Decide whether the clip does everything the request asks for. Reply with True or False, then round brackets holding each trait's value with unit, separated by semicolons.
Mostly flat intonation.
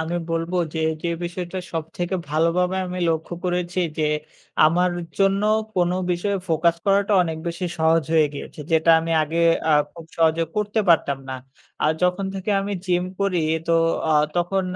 True (2.0 semitones)